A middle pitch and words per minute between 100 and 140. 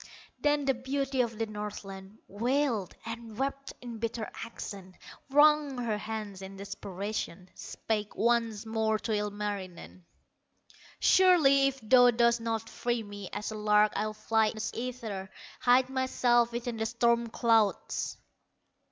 No: high, 225 Hz; slow, 135 wpm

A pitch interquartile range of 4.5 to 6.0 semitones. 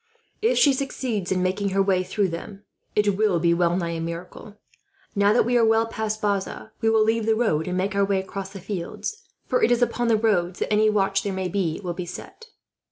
No: average, 3.2 semitones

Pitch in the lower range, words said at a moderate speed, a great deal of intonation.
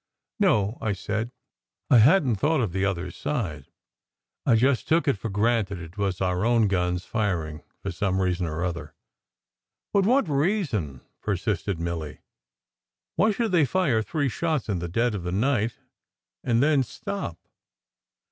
Yes: low, 105 Hz; average, 155 wpm; wide, 7.4 semitones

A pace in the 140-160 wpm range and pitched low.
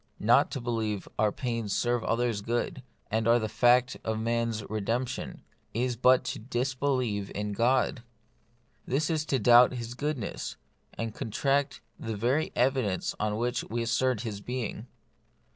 Yes: average, 150 wpm; low, 120 Hz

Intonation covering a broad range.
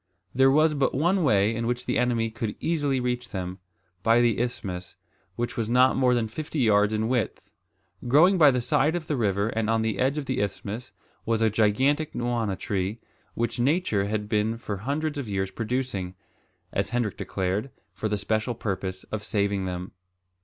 No: average, 4.1 semitones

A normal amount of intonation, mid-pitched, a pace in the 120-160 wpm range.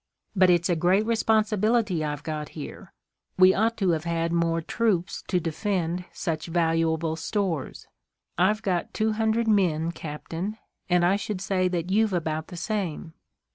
Yes: average, 4.1 semitones; medium, 180 Hz; average, 155 wpm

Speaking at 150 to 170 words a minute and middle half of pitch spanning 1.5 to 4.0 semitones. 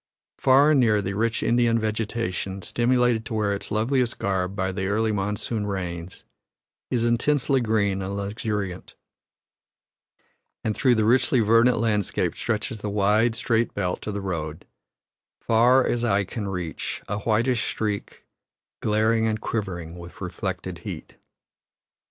No: average, 140 wpm; average, 2.9 semitones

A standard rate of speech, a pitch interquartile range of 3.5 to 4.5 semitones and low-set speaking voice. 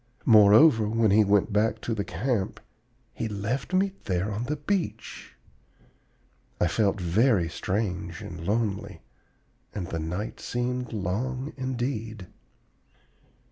No: slow, 120 wpm; average, 4.1 semitones; low, 110 Hz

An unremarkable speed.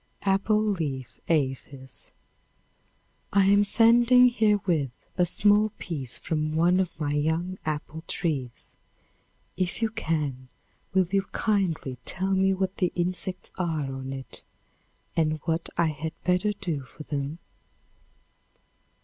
No: slow, 125 wpm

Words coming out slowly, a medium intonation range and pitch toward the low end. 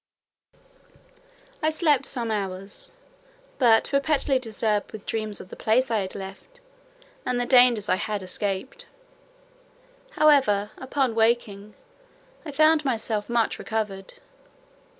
No: slow, 115 wpm; average, 4.7 semitones; high, 225 Hz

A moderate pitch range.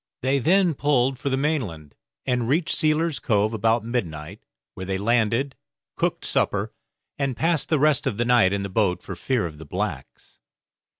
No: wide, 5.8 semitones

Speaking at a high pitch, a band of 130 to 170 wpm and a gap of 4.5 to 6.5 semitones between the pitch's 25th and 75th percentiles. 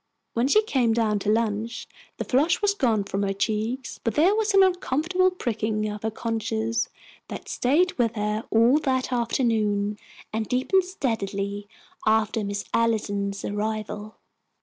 No: high, 225 Hz; average, 150 wpm; average, 3.8 semitones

